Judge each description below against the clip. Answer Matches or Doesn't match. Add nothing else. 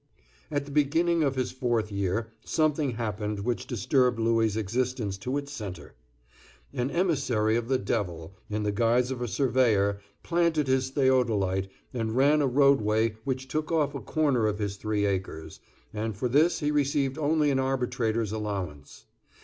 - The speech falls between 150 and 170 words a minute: Matches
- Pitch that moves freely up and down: Doesn't match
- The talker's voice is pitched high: Doesn't match